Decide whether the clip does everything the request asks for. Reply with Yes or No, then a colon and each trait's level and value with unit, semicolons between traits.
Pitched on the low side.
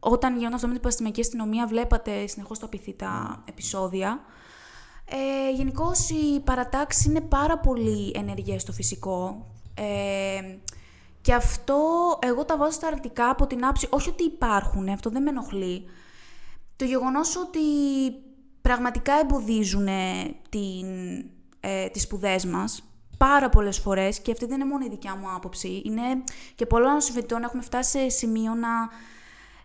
No: high, 235 Hz